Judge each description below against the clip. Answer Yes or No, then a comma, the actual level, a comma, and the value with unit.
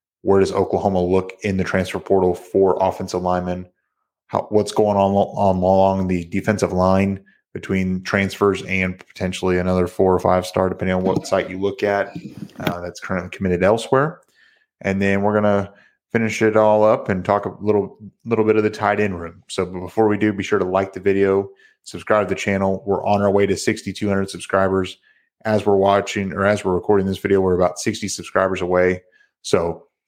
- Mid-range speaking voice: No, very low, 95 Hz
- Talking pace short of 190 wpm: No, average, 195 wpm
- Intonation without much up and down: Yes, narrow, 1.5 semitones